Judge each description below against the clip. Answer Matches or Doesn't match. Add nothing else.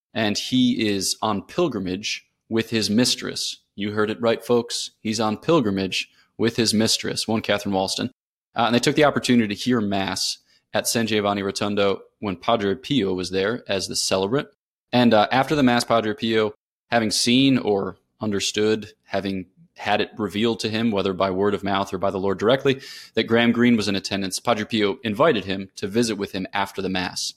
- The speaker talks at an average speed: Matches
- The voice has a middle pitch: Doesn't match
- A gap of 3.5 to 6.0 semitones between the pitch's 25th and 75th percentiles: Doesn't match